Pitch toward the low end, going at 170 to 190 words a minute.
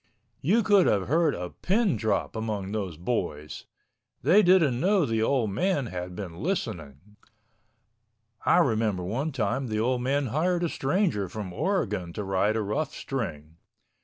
No: low, 115 Hz; average, 155 wpm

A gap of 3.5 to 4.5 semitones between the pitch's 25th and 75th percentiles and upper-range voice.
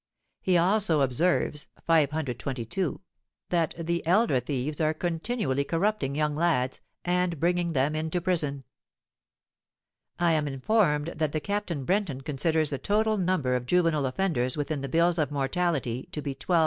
No: average, 4.1 semitones; medium, 160 Hz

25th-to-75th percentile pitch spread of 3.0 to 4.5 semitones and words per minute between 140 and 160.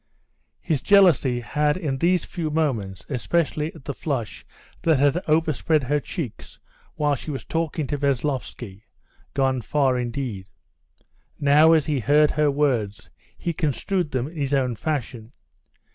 Yes: average, 3.4 semitones; average, 145 wpm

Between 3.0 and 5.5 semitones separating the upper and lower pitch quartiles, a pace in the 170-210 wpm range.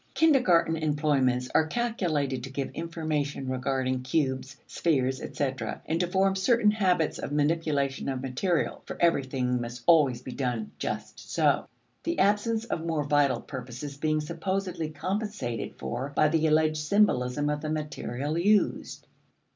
No: average, 4.5 semitones; average, 140 wpm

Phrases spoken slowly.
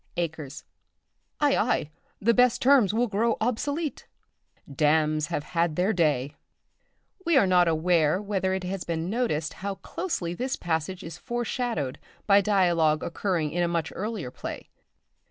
No: average, 145 wpm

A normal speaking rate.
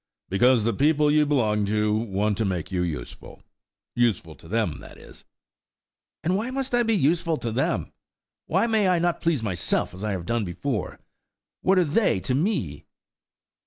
Yes: average, 170 wpm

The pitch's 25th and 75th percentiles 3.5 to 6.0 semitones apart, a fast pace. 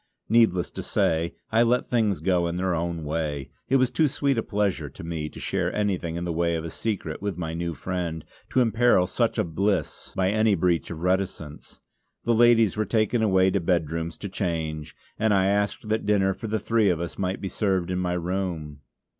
Yes: average, 4.1 semitones; fast, 210 wpm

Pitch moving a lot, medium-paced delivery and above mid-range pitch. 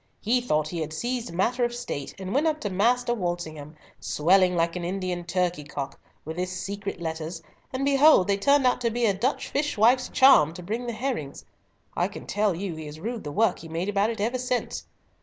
No: wide, 6.2 semitones; fast, 215 wpm; high, 195 Hz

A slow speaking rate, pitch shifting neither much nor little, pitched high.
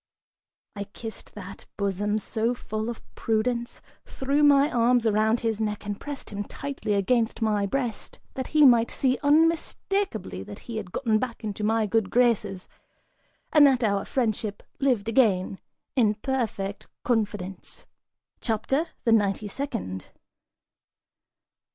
Yes: slow, 130 wpm; average, 3.6 semitones; high, 225 Hz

